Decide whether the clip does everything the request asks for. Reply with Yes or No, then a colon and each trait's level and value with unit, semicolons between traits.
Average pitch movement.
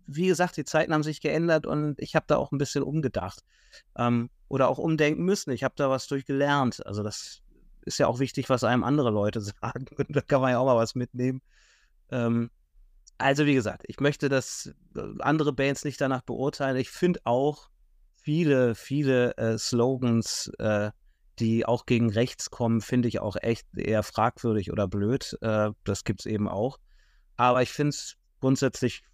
Yes: average, 3.8 semitones